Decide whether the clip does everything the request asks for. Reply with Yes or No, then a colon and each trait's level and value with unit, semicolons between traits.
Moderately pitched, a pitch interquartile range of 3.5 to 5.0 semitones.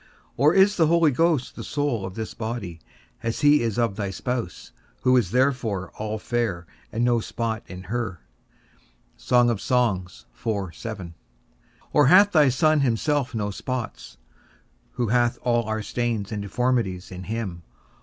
No: low, 115 Hz; average, 4.3 semitones